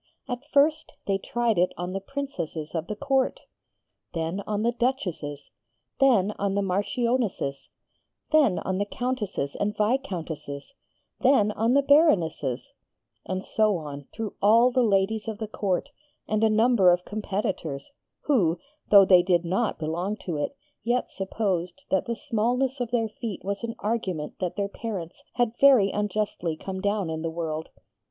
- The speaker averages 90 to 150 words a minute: No, average, 160 wpm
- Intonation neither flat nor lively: Yes, average, 5.0 semitones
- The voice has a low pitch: No, high, 205 Hz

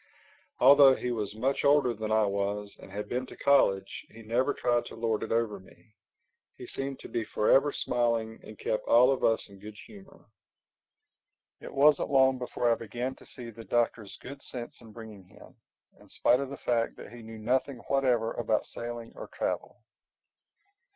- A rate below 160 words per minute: No, average, 180 wpm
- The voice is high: No, low, 120 Hz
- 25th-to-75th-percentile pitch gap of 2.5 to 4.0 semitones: Yes, average, 3.2 semitones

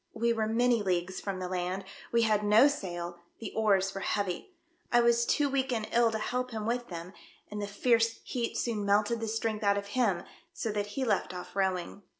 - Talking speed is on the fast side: Yes, fast, 210 wpm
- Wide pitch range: No, average, 3.2 semitones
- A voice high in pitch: Yes, high, 215 Hz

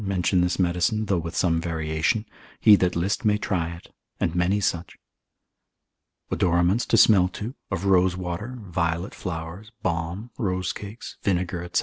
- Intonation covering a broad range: No, average, 3.0 semitones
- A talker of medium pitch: No, very low, 90 Hz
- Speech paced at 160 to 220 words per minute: No, average, 150 wpm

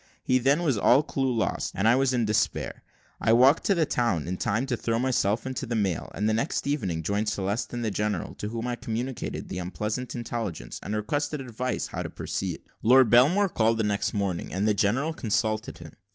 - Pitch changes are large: No, average, 3.8 semitones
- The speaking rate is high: Yes, fast, 210 wpm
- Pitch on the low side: Yes, low, 115 Hz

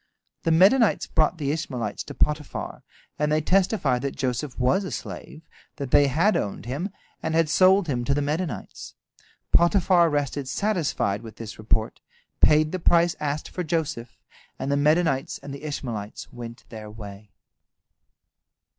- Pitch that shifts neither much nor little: Yes, average, 5.0 semitones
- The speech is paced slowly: No, average, 155 wpm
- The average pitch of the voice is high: No, medium, 145 Hz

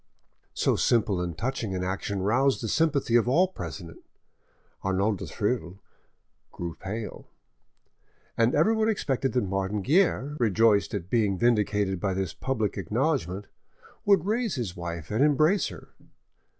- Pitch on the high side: No, low, 110 Hz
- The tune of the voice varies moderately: No, wide, 6.1 semitones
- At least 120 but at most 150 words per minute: Yes, slow, 135 wpm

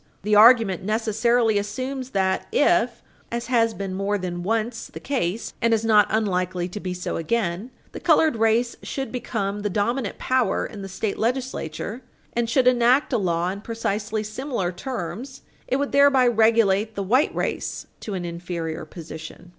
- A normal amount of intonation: Yes, average, 4.0 semitones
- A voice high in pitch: Yes, high, 215 Hz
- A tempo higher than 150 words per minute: Yes, average, 165 wpm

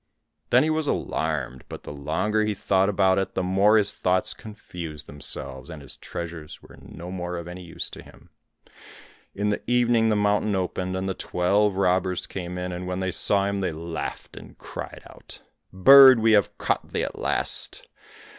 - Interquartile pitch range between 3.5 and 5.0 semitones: No, average, 2.9 semitones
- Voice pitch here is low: Yes, very low, 95 Hz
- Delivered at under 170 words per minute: No, average, 185 wpm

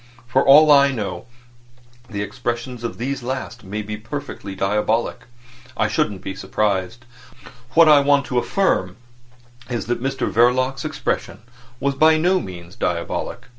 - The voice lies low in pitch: Yes, low, 120 Hz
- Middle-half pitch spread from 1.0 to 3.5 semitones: No, average, 5.0 semitones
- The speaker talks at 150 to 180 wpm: No, average, 140 wpm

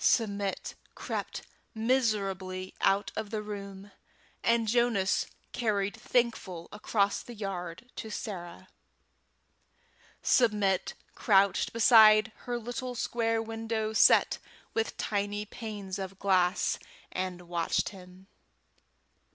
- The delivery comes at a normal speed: No, slow, 100 wpm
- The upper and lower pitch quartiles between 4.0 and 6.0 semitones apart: No, average, 2.8 semitones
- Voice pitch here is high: Yes, high, 205 Hz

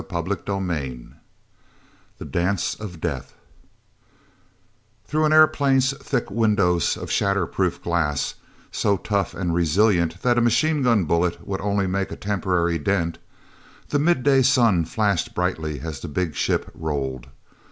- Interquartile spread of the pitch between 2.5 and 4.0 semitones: No, average, 4.7 semitones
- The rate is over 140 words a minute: No, slow, 135 wpm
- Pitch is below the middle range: Yes, very low, 95 Hz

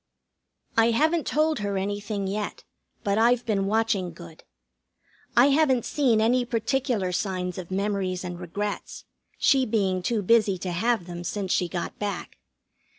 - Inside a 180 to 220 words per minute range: No, average, 150 wpm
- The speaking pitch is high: Yes, high, 205 Hz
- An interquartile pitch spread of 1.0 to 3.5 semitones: No, average, 4.2 semitones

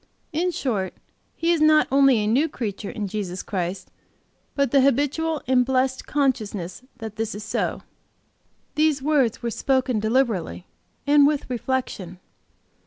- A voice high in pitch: Yes, very high, 255 Hz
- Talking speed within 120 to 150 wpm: Yes, average, 140 wpm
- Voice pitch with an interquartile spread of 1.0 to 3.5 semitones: No, average, 5.3 semitones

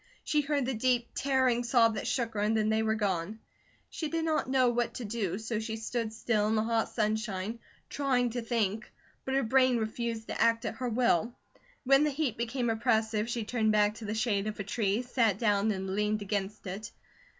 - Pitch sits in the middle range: No, high, 225 Hz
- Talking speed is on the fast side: Yes, fast, 210 wpm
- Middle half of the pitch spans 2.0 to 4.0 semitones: Yes, narrow, 2.5 semitones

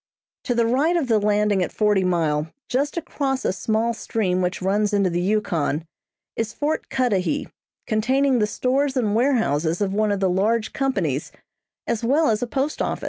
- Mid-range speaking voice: No, high, 215 Hz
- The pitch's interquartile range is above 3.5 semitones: Yes, average, 5.2 semitones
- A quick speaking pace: No, average, 180 wpm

